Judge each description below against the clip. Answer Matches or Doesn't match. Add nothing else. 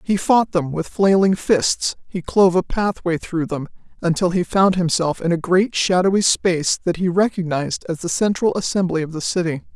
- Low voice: Doesn't match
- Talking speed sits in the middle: Matches